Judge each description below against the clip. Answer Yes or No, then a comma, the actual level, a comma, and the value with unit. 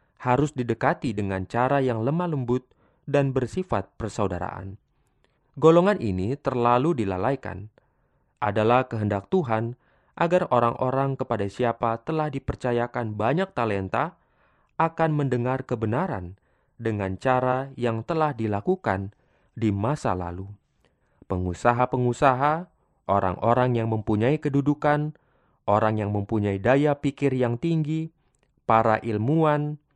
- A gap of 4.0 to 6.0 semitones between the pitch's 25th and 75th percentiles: Yes, average, 4.8 semitones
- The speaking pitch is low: Yes, low, 125 Hz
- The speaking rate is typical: Yes, average, 100 wpm